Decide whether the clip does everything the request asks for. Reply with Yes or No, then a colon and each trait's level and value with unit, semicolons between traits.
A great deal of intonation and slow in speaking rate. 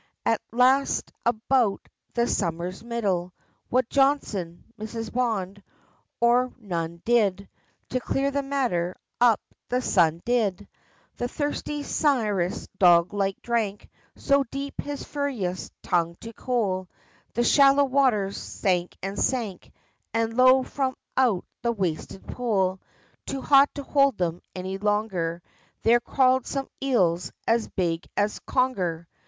Yes: wide, 5.7 semitones; slow, 125 wpm